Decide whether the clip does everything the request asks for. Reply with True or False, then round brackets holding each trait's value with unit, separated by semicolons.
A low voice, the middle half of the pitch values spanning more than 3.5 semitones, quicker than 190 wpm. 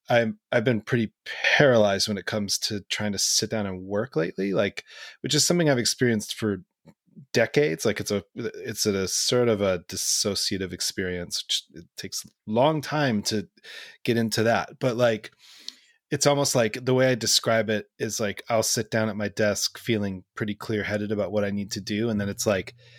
False (110 Hz; 3.2 semitones; 200 wpm)